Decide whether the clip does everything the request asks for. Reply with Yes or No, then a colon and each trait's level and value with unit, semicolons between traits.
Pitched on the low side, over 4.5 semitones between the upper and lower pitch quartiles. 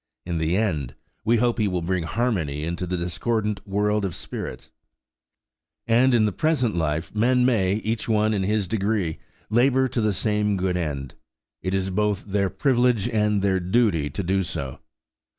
No: low, 100 Hz; average, 3.9 semitones